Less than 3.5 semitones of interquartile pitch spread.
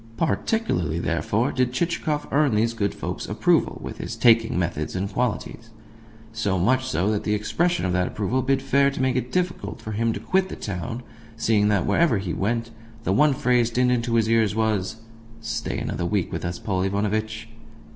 No: average, 4.1 semitones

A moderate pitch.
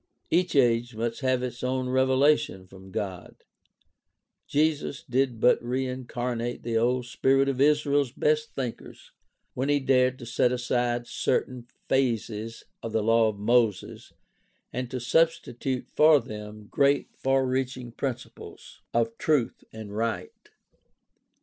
No: low, 125 Hz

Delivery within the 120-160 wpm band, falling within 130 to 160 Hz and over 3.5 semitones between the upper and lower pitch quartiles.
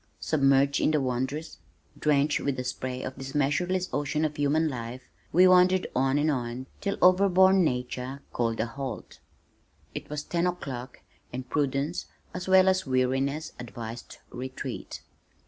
Yes: average, 145 wpm; medium, 140 Hz; average, 4.1 semitones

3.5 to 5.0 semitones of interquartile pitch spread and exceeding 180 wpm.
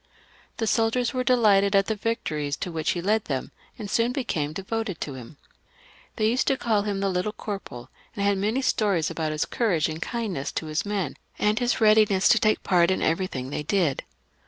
No: wide, 5.4 semitones; average, 200 wpm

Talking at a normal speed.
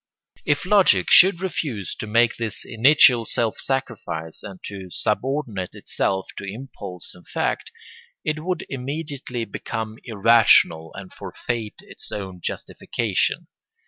No: slow, 125 wpm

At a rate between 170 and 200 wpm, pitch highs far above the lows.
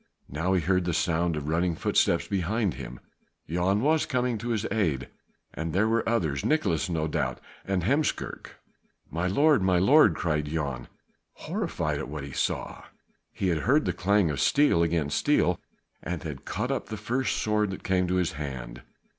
Yes: average, 180 wpm; wide, 5.7 semitones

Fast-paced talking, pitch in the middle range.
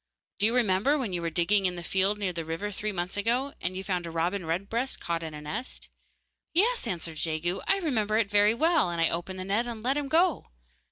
No: fast, 230 wpm; high, 200 Hz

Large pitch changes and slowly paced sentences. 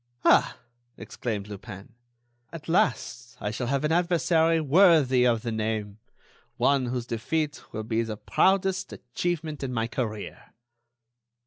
Yes: wide, 6.4 semitones; slow, 125 wpm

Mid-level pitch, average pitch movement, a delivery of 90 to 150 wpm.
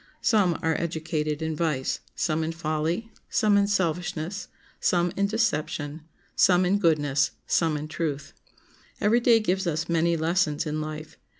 Yes: medium, 165 Hz; average, 3.4 semitones; average, 145 wpm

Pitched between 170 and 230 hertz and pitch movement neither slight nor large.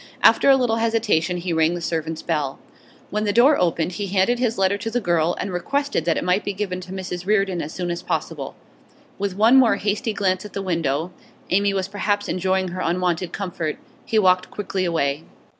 Yes: medium, 185 Hz; average, 3.2 semitones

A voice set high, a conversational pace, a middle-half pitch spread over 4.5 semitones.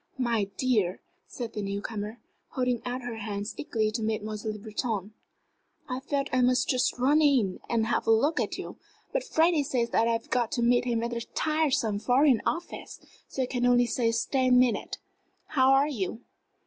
No: high, 240 Hz; average, 185 wpm; average, 2.9 semitones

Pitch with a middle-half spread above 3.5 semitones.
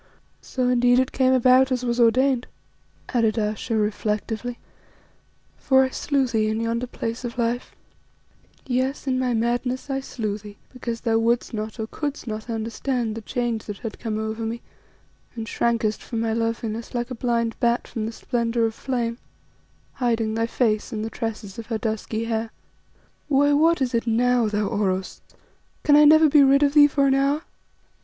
No: narrow, 2.5 semitones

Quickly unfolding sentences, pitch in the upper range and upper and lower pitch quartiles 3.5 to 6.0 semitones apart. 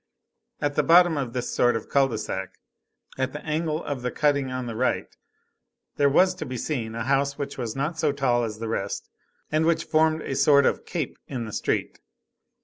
No: fast, 210 wpm; medium, 140 Hz; average, 4.0 semitones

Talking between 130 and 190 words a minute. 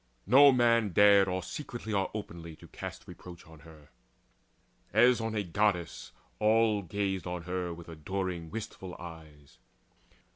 Yes: average, 140 wpm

